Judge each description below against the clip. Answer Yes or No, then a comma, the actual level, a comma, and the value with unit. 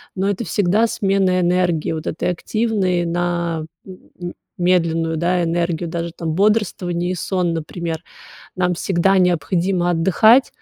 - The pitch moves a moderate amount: No, narrow, 2.0 semitones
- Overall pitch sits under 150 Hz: No, medium, 175 Hz